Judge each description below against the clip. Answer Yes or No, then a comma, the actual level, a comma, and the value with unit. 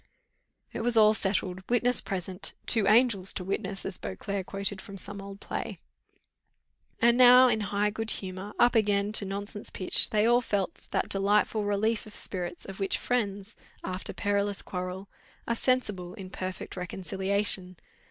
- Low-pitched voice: No, high, 200 Hz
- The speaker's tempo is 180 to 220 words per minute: No, average, 155 wpm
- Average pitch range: No, narrow, 2.3 semitones